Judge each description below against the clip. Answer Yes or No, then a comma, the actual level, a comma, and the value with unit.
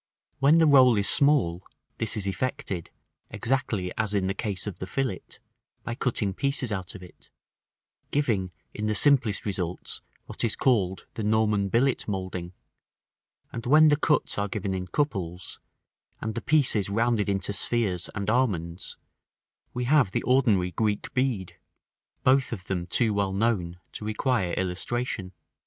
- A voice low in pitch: Yes, low, 105 Hz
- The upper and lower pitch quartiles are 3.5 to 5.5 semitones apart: Yes, average, 4.9 semitones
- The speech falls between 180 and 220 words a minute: No, average, 150 wpm